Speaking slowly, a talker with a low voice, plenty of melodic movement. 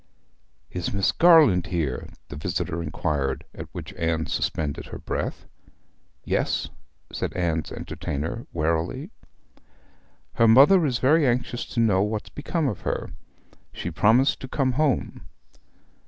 Yes: slow, 125 wpm; low, 100 Hz; wide, 8.1 semitones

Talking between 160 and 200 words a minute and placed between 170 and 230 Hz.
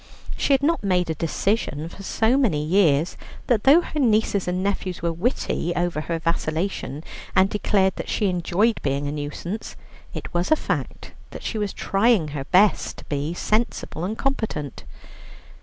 Yes: average, 170 wpm; medium, 185 Hz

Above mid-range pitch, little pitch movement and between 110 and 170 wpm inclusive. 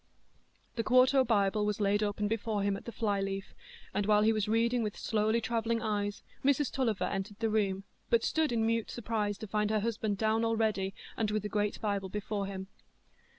No: high, 215 Hz; narrow, 1.9 semitones; average, 195 wpm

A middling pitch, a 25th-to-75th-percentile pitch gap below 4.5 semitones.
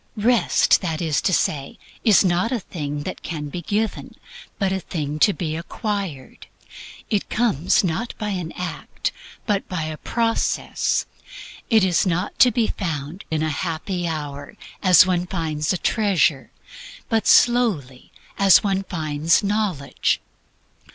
No: medium, 180 Hz; average, 4.8 semitones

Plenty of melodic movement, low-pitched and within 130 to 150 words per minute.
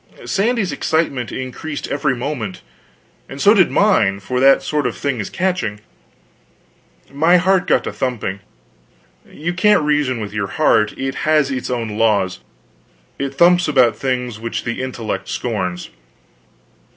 Yes: wide, 5.8 semitones; low, 130 Hz; average, 140 wpm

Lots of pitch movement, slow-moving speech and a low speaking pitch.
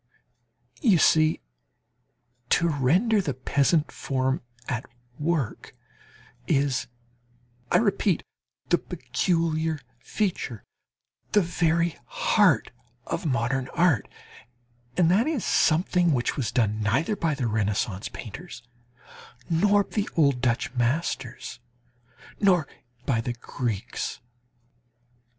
No: wide, 6.1 semitones; slow, 100 wpm; medium, 150 Hz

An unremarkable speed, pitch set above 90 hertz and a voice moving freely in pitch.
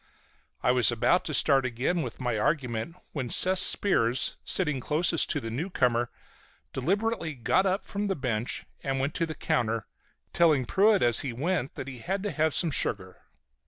Yes: average, 175 wpm; medium, 140 Hz; wide, 6.5 semitones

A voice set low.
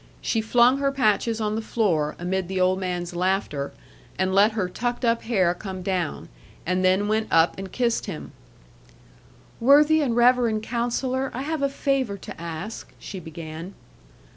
No: high, 210 Hz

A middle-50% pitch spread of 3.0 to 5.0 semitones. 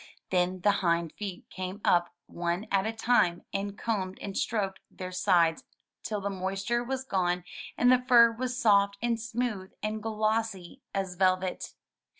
Yes: average, 3.5 semitones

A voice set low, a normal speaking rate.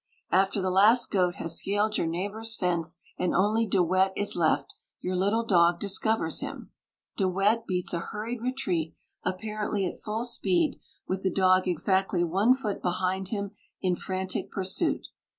No: high, 190 Hz; average, 160 wpm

